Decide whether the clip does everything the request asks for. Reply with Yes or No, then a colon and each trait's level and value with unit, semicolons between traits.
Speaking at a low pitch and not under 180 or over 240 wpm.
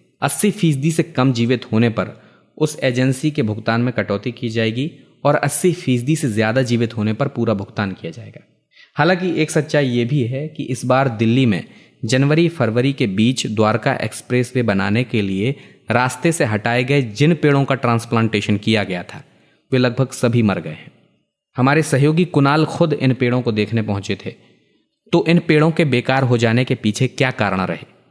Yes: low, 130 Hz; average, 185 wpm